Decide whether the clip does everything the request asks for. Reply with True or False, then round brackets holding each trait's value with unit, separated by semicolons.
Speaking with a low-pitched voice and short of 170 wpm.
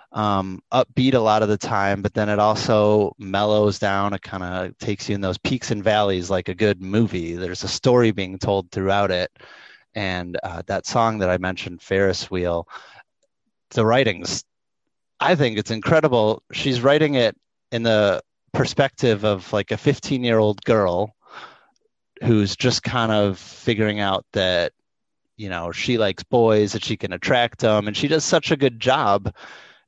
False (105 Hz; 175 wpm)